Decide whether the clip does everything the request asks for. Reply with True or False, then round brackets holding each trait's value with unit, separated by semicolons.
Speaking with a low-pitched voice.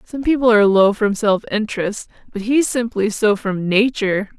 False (215 Hz)